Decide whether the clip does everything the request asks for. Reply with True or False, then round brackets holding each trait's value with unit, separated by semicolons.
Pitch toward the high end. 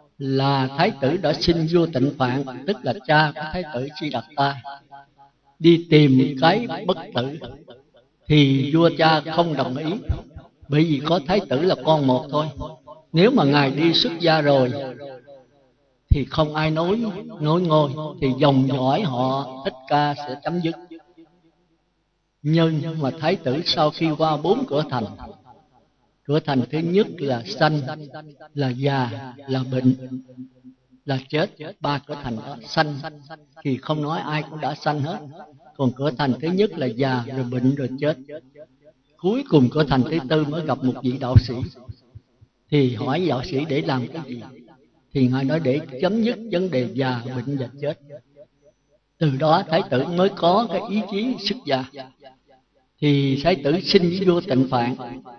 False (145 Hz)